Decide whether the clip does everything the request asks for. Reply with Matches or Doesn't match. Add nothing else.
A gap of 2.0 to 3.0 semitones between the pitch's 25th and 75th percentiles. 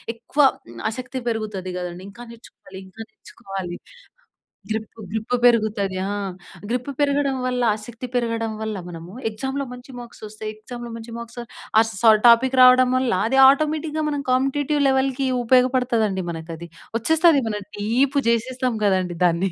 Doesn't match